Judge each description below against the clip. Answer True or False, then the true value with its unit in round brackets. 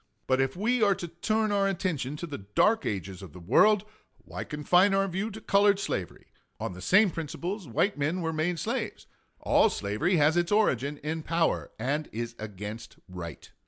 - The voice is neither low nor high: True (160 Hz)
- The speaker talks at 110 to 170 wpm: False (185 wpm)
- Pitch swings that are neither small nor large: False (8.8 semitones)